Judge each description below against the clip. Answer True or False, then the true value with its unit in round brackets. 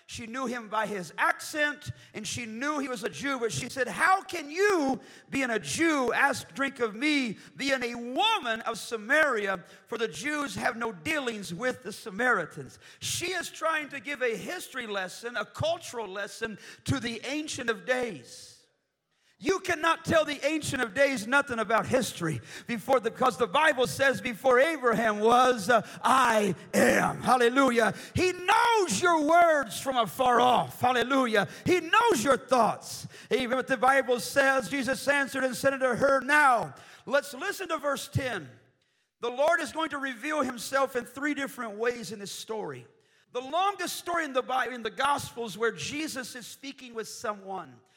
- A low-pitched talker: False (255 Hz)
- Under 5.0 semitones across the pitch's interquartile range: True (4.0 semitones)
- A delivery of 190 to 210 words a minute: False (170 wpm)